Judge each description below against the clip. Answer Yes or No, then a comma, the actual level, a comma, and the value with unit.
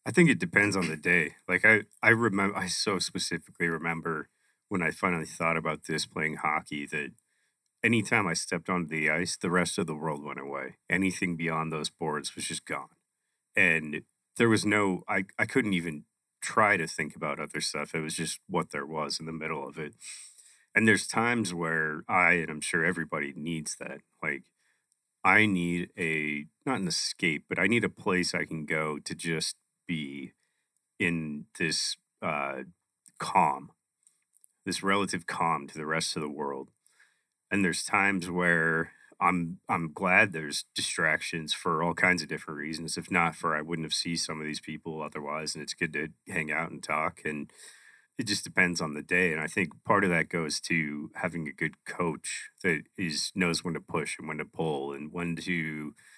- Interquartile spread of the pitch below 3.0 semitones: Yes, narrow, 2.5 semitones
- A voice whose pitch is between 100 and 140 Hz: No, very low, 80 Hz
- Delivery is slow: No, average, 190 wpm